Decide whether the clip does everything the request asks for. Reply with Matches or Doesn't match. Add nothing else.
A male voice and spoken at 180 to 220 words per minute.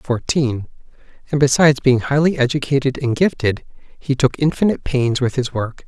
Doesn't match